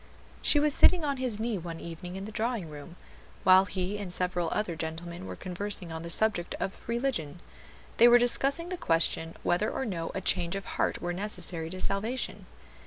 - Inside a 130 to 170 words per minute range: No, average, 190 wpm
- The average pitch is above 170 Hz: Yes, high, 190 Hz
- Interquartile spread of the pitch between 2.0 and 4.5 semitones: No, average, 5.0 semitones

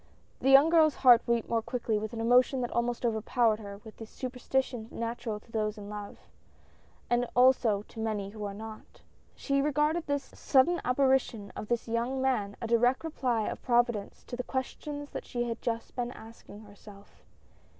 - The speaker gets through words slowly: No, average, 180 wpm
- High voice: Yes, high, 235 Hz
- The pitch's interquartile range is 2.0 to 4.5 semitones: Yes, average, 3.1 semitones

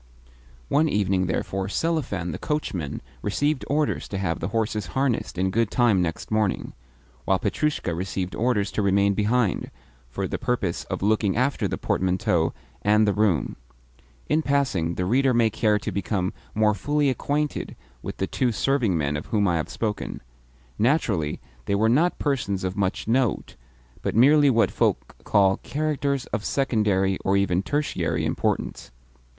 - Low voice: Yes, low, 105 Hz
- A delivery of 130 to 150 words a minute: No, average, 160 wpm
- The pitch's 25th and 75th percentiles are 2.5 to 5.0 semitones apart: No, wide, 5.5 semitones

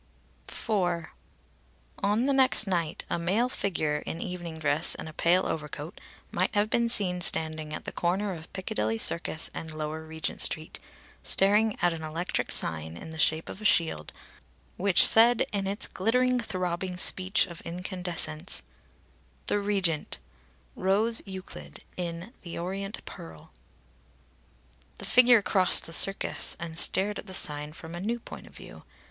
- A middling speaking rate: Yes, average, 155 wpm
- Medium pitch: Yes, medium, 180 Hz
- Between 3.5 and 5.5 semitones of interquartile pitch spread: Yes, average, 4.1 semitones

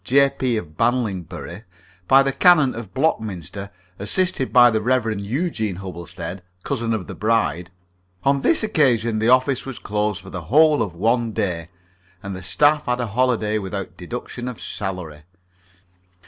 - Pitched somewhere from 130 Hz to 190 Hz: No, low, 110 Hz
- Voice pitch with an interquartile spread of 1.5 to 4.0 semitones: No, average, 5.1 semitones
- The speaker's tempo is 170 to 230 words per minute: No, average, 150 wpm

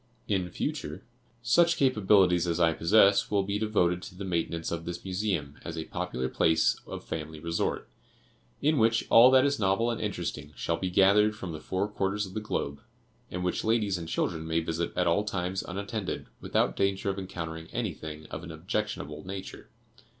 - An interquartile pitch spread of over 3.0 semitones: Yes, average, 4.0 semitones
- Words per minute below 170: No, average, 180 wpm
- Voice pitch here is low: Yes, very low, 95 Hz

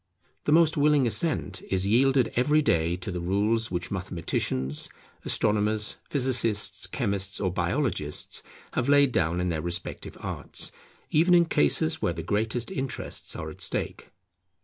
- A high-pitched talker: No, low, 105 Hz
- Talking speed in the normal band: Yes, average, 145 wpm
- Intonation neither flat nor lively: No, wide, 7.3 semitones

